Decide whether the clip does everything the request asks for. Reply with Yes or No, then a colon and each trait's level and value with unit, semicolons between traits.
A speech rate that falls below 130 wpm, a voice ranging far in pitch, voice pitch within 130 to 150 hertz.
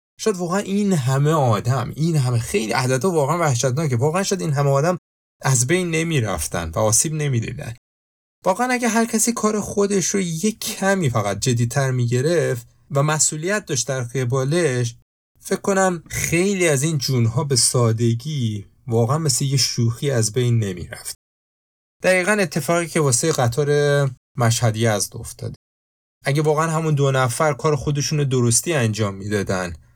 No: fast, 155 wpm; wide, 5.9 semitones; medium, 140 Hz